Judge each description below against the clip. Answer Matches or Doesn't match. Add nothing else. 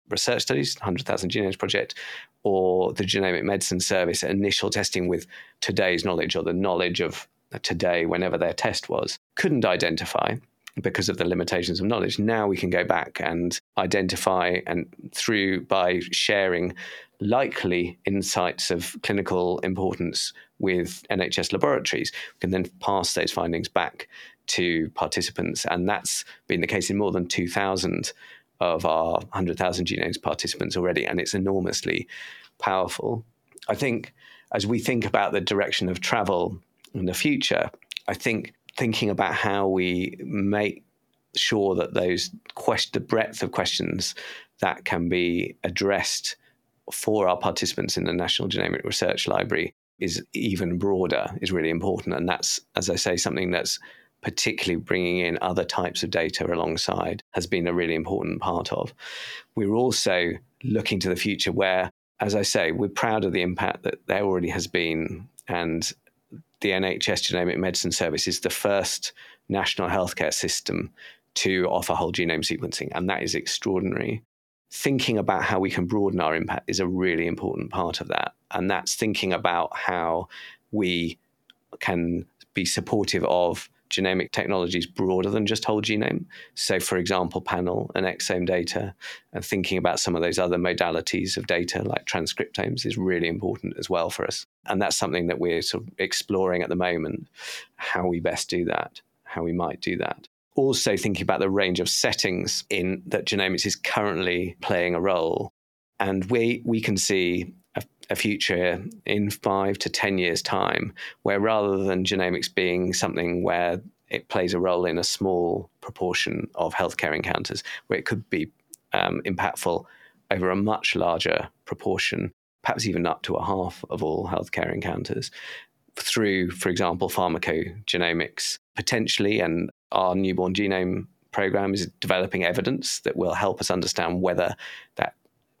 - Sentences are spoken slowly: Doesn't match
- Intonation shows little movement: Matches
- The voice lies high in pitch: Doesn't match